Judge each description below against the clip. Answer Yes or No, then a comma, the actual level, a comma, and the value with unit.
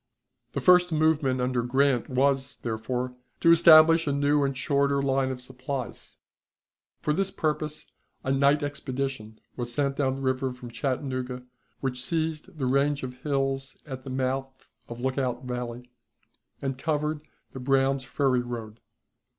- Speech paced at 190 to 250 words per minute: No, average, 145 wpm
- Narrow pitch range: Yes, narrow, 2.2 semitones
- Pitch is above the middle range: No, low, 135 Hz